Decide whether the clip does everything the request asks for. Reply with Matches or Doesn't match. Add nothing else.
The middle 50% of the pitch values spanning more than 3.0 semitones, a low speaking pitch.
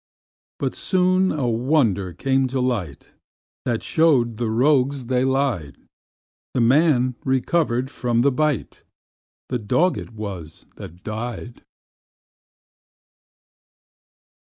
Matches